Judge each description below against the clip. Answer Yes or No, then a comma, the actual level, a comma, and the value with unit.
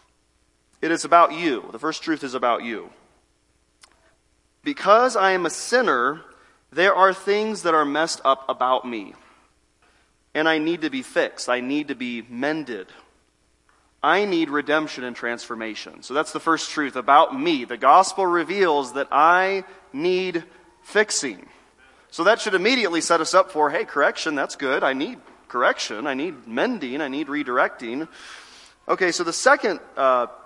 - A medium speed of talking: Yes, average, 160 wpm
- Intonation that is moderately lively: No, wide, 7.5 semitones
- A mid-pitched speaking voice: Yes, medium, 155 Hz